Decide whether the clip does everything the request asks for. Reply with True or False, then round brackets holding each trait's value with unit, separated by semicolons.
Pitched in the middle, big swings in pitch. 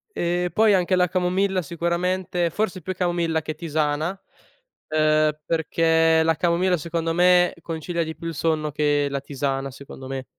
False (165 Hz; 2.7 semitones)